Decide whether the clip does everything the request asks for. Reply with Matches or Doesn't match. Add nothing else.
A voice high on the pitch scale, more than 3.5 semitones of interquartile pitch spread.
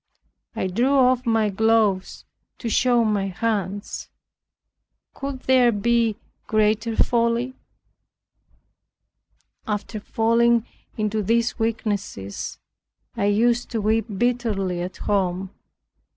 Doesn't match